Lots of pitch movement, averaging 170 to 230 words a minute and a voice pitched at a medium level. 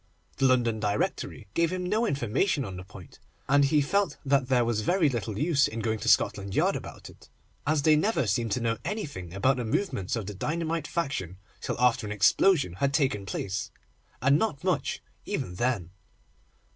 No: wide, 6.8 semitones; average, 185 wpm; low, 130 Hz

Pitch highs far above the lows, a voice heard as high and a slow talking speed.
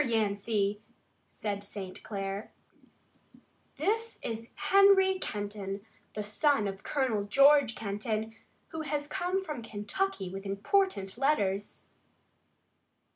Yes: wide, 6.8 semitones; high, 220 Hz; slow, 100 wpm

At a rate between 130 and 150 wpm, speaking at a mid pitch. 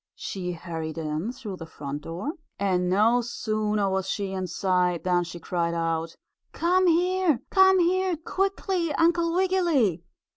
No: average, 140 wpm; high, 200 Hz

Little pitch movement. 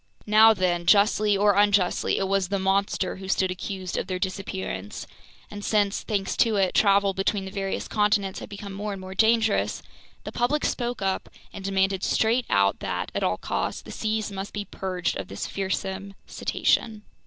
Yes: narrow, 1.6 semitones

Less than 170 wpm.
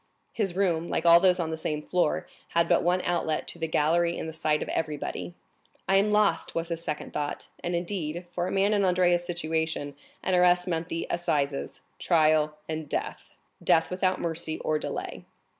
No: average, 185 wpm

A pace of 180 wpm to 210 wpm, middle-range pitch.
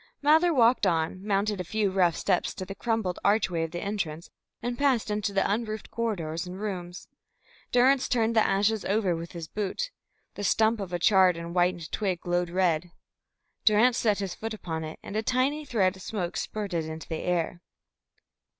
No: average, 185 wpm; high, 195 Hz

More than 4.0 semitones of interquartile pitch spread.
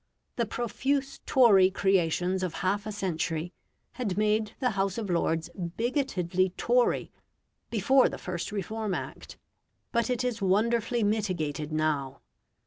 Yes: average, 4.6 semitones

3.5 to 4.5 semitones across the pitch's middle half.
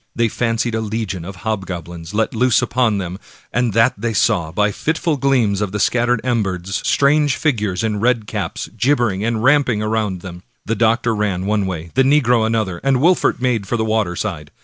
Yes: average, 3.9 semitones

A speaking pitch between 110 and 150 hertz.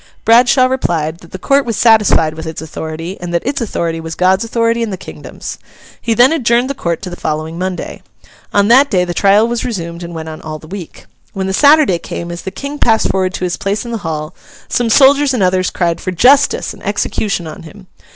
No: high, 190 Hz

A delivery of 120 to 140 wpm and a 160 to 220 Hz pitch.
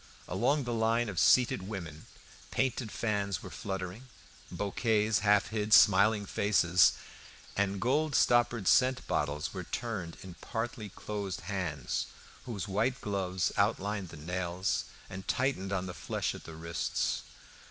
No: slow, 135 wpm; low, 100 Hz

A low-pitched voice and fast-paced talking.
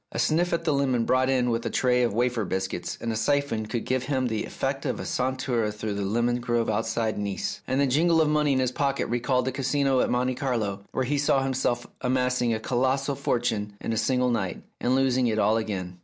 Yes: low, 125 Hz; fast, 230 wpm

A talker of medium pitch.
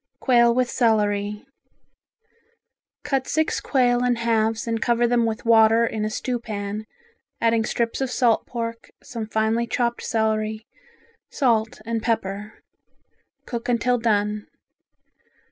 No: high, 230 Hz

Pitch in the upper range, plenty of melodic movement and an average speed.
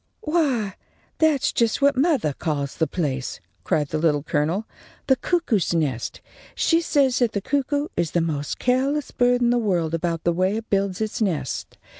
Yes: high, 200 Hz; wide, 8.3 semitones; average, 180 wpm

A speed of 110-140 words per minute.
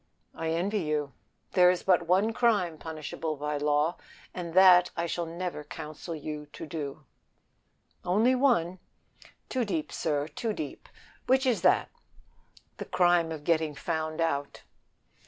Yes: slow, 135 wpm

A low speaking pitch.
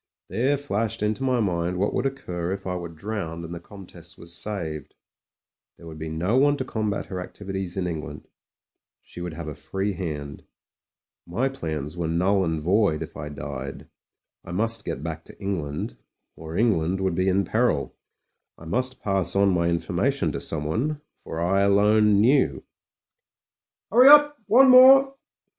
Yes: very low, 95 Hz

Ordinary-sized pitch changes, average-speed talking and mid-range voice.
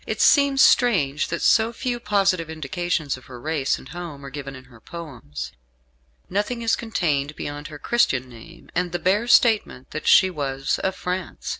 No: wide, 6.5 semitones; average, 175 wpm; medium, 165 Hz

